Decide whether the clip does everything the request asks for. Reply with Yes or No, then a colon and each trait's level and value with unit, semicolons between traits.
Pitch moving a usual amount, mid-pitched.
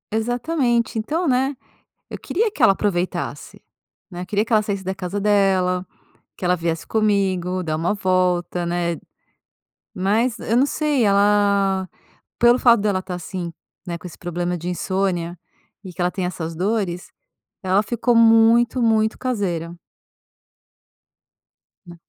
No: average, 4.0 semitones; high, 195 Hz